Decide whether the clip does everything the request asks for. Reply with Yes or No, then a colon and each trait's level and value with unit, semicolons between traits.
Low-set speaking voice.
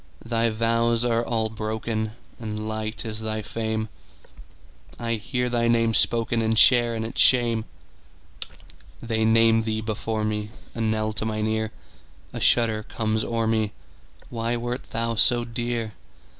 Yes: low, 115 Hz